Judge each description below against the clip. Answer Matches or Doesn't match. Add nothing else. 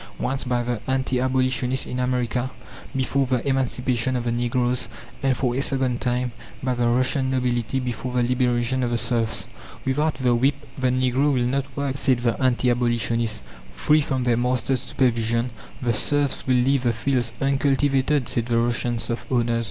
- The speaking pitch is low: Matches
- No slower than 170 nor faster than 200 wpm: Matches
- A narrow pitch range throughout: Matches